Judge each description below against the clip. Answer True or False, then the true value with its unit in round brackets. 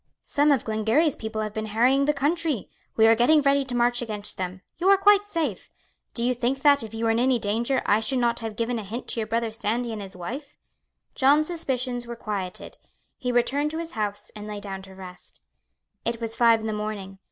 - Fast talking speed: True (225 wpm)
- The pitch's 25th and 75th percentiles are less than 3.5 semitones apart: False (4.2 semitones)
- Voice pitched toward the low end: False (235 Hz)